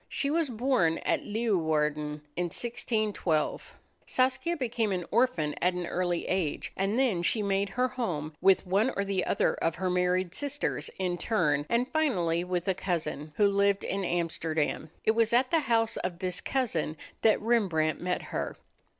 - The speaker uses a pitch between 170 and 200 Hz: Yes, high, 190 Hz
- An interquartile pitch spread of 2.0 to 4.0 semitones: No, average, 5.3 semitones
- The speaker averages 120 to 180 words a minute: Yes, average, 165 wpm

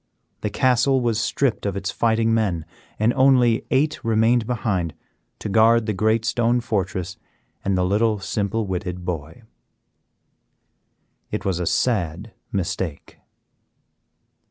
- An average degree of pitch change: Yes, average, 3.8 semitones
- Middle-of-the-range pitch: No, low, 110 Hz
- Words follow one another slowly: Yes, slow, 125 wpm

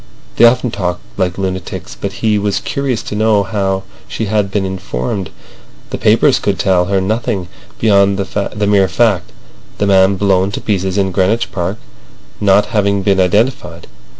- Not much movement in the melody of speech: Yes, narrow, 1.8 semitones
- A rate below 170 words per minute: Yes, average, 160 wpm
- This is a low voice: Yes, low, 100 Hz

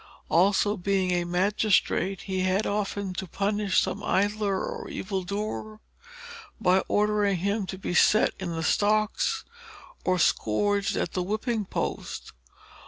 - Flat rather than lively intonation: Yes, narrow, 2.1 semitones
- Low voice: No, high, 200 Hz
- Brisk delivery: No, slow, 135 wpm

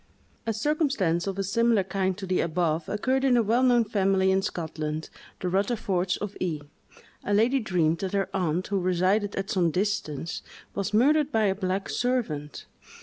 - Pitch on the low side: No, high, 195 Hz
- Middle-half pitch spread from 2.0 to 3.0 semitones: No, average, 3.5 semitones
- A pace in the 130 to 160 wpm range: No, average, 175 wpm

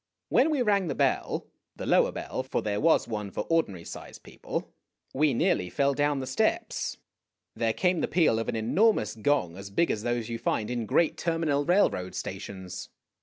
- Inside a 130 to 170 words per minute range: No, average, 185 wpm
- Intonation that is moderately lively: No, wide, 7.7 semitones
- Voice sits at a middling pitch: No, low, 130 Hz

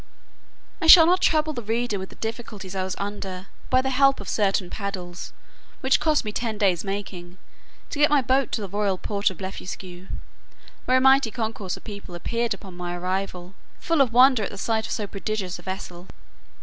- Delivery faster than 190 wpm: Yes, average, 200 wpm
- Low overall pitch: No, high, 205 Hz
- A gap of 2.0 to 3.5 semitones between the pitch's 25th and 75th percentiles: No, average, 4.8 semitones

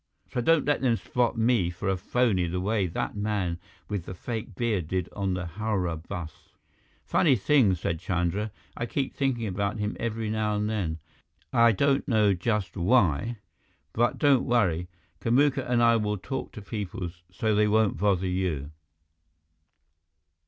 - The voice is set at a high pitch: No, low, 105 Hz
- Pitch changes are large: No, average, 4.3 semitones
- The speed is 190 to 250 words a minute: No, average, 160 wpm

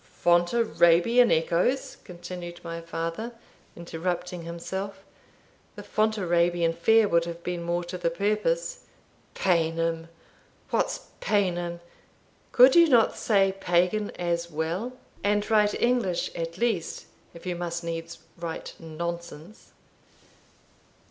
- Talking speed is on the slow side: Yes, slow, 110 wpm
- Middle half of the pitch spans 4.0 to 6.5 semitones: No, average, 3.3 semitones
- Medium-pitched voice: Yes, medium, 175 Hz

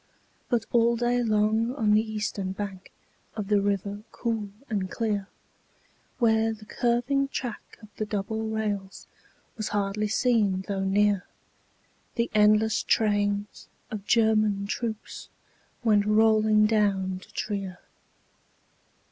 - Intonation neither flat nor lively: No, narrow, 1.6 semitones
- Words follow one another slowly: Yes, slow, 120 wpm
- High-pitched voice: Yes, high, 215 Hz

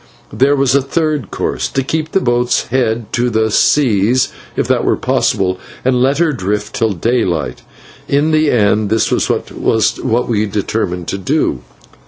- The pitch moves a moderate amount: Yes, average, 4.9 semitones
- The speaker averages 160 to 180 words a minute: Yes, average, 165 wpm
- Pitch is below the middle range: Yes, low, 120 Hz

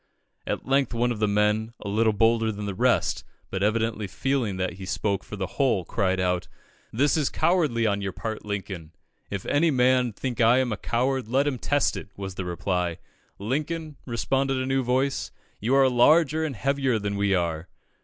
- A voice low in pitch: Yes, low, 115 Hz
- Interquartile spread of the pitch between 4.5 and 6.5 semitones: Yes, average, 4.9 semitones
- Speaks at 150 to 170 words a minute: No, average, 195 wpm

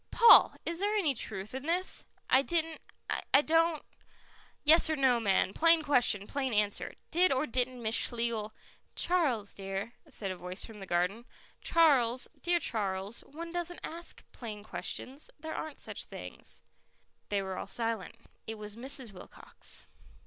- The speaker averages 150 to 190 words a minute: Yes, average, 160 wpm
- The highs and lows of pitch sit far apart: Yes, wide, 7.3 semitones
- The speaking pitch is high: Yes, very high, 250 Hz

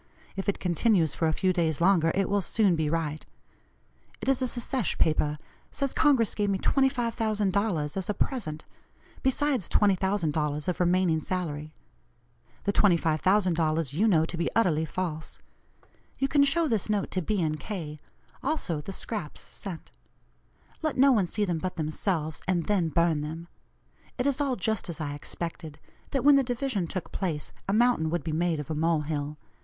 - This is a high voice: No, medium, 180 Hz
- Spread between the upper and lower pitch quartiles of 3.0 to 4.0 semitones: No, wide, 5.4 semitones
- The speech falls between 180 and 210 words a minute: No, average, 170 wpm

